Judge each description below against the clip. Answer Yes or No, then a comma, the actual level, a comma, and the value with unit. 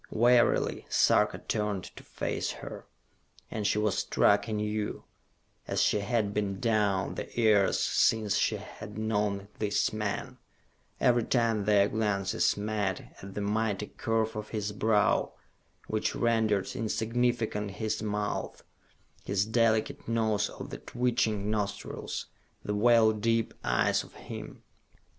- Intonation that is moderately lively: No, narrow, 1.5 semitones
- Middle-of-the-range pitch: No, low, 105 Hz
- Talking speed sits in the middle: No, slow, 130 wpm